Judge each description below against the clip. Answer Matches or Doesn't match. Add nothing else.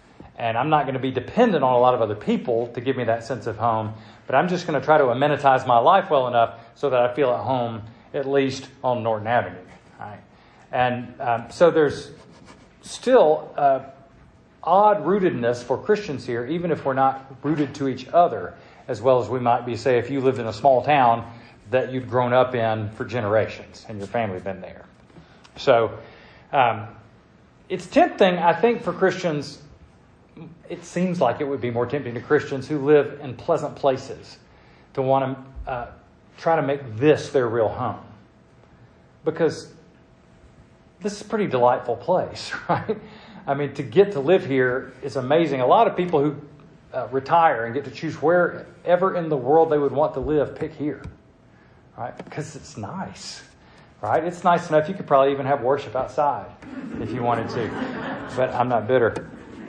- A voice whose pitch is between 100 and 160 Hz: Matches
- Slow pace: Doesn't match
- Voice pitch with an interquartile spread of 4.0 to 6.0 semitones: Matches